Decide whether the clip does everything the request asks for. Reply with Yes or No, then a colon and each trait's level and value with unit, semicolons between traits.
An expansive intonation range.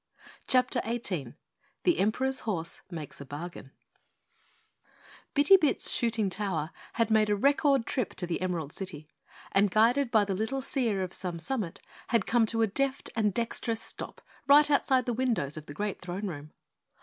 Yes: wide, 5.9 semitones